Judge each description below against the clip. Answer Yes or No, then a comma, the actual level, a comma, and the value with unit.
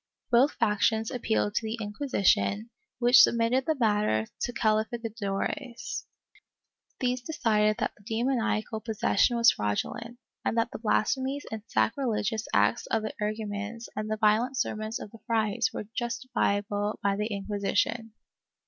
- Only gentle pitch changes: Yes, narrow, 2.3 semitones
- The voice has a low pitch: No, high, 220 Hz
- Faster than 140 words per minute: No, slow, 135 wpm